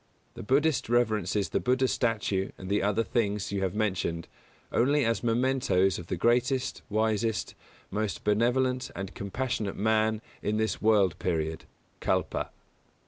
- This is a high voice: No, low, 110 Hz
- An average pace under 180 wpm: Yes, average, 140 wpm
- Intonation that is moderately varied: Yes, average, 3.6 semitones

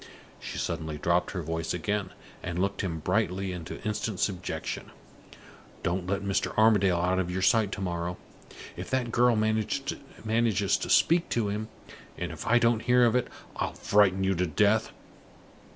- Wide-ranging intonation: No, average, 3.7 semitones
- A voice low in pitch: Yes, low, 100 Hz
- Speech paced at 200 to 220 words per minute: No, average, 165 wpm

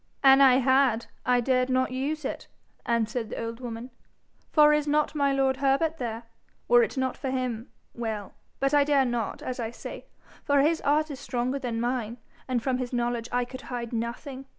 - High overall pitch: Yes, very high, 255 Hz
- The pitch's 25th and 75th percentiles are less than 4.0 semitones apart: Yes, narrow, 2.5 semitones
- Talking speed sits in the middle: Yes, average, 195 wpm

